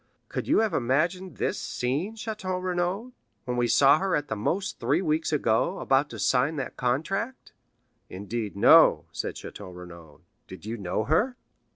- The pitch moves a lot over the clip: Yes, wide, 8.2 semitones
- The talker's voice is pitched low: No, medium, 145 Hz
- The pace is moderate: Yes, average, 165 wpm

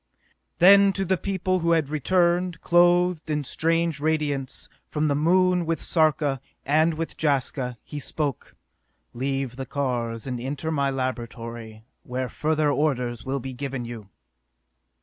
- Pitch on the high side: No, medium, 145 Hz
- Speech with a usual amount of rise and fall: Yes, average, 4.2 semitones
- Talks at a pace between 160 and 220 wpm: No, average, 140 wpm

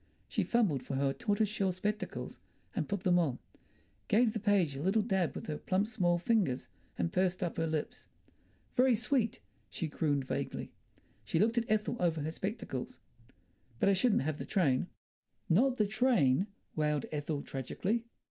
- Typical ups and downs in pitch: No, wide, 6.1 semitones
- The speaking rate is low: No, average, 165 wpm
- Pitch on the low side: No, medium, 185 Hz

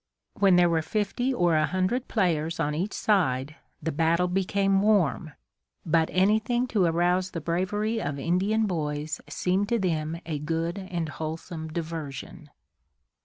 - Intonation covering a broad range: No, average, 3.7 semitones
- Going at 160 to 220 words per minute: No, average, 145 wpm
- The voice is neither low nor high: Yes, medium, 175 Hz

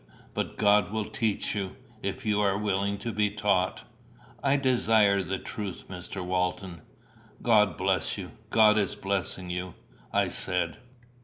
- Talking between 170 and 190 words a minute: No, average, 145 wpm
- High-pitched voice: No, low, 100 Hz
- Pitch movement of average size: No, narrow, 2.3 semitones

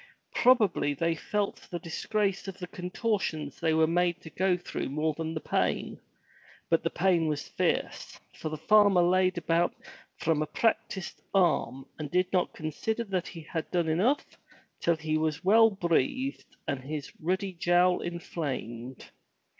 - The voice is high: No, medium, 175 Hz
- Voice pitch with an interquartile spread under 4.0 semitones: Yes, average, 3.3 semitones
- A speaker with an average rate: Yes, average, 160 wpm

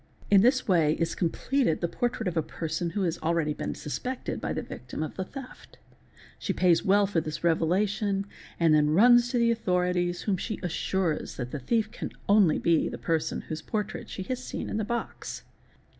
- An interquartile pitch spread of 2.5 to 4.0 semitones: No, average, 4.8 semitones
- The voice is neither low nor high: Yes, medium, 180 Hz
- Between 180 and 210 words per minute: Yes, average, 195 wpm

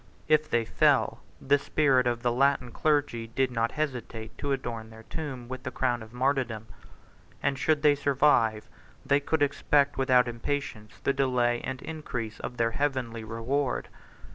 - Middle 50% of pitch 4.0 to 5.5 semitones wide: No, average, 3.4 semitones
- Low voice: Yes, low, 130 Hz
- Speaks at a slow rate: No, average, 165 wpm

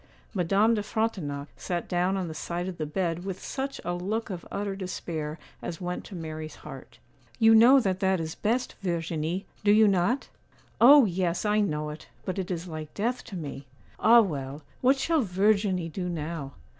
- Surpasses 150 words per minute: Yes, average, 185 wpm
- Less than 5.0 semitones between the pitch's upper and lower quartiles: Yes, average, 4.4 semitones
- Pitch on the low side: No, medium, 185 Hz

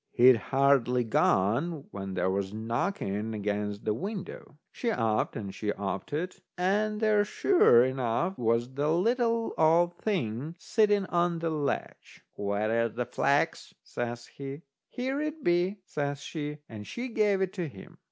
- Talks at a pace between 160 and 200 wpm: No, average, 150 wpm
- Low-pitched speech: No, medium, 145 Hz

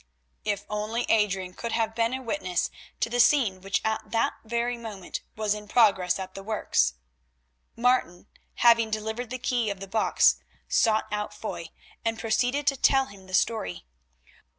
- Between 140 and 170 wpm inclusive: Yes, average, 165 wpm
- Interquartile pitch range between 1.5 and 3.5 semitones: Yes, average, 3.2 semitones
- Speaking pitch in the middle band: No, high, 220 Hz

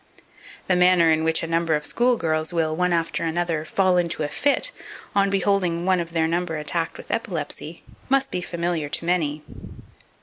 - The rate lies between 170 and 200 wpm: Yes, average, 180 wpm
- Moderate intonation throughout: No, narrow, 2.1 semitones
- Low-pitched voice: No, medium, 170 Hz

